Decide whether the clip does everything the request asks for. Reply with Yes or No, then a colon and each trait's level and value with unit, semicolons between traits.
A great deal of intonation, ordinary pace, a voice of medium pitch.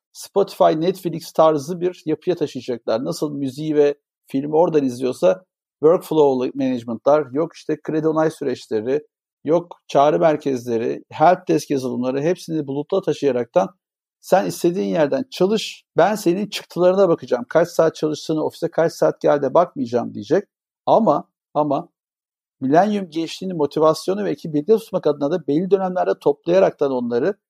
No: average, 4.2 semitones; average, 130 wpm; medium, 160 Hz